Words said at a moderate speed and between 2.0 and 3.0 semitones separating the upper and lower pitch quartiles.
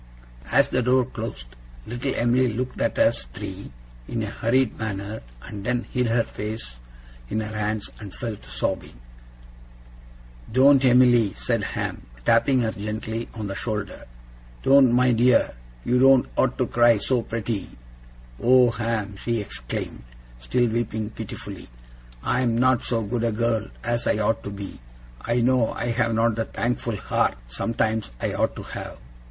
Yes: average, 160 wpm; narrow, 2.4 semitones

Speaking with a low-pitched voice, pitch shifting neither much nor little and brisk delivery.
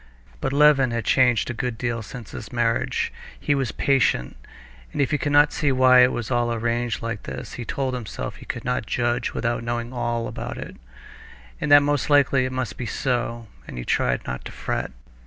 No: low, 120 Hz; narrow, 2.1 semitones; fast, 210 wpm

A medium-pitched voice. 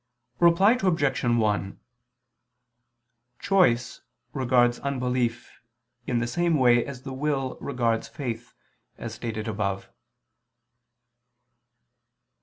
No: low, 125 Hz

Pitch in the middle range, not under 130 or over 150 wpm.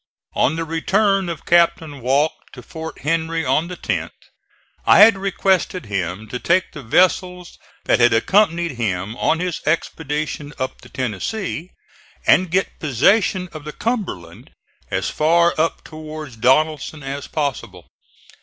Yes: medium, 155 Hz; average, 140 wpm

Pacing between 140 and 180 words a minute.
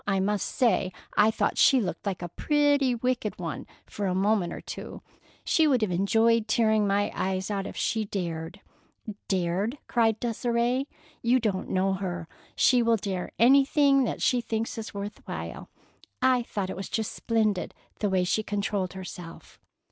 Yes: average, 170 wpm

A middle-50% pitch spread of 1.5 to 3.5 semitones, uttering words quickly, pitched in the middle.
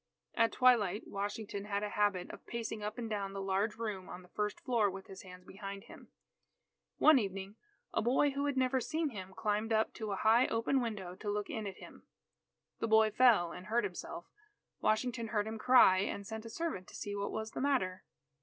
No: average, 2.8 semitones; fast, 210 wpm; high, 210 Hz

